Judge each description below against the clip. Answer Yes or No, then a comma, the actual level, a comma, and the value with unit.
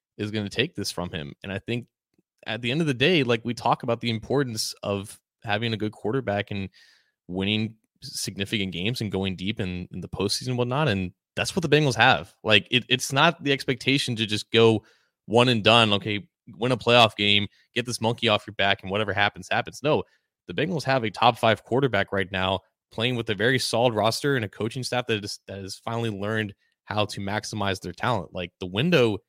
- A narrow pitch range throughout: No, average, 3.6 semitones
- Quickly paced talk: Yes, fast, 220 wpm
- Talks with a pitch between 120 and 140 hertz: No, low, 110 Hz